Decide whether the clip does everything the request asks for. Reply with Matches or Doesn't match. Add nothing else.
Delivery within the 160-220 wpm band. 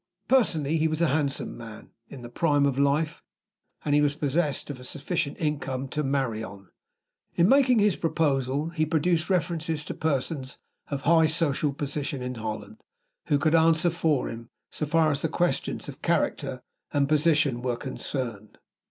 Matches